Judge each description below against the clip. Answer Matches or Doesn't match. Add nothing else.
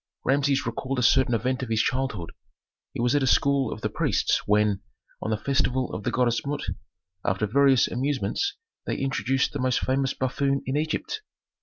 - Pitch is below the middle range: Matches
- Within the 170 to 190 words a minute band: Matches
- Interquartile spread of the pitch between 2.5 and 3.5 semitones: Matches